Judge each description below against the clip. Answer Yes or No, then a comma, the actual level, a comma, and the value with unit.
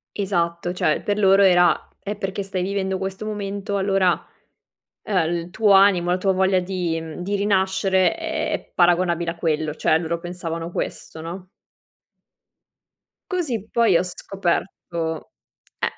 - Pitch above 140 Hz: Yes, medium, 185 Hz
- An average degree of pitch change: No, narrow, 2.3 semitones